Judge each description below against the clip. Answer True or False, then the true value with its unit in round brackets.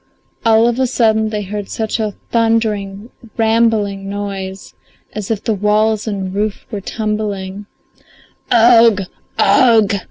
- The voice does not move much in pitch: True (2.0 semitones)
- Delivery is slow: True (130 wpm)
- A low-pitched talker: False (215 Hz)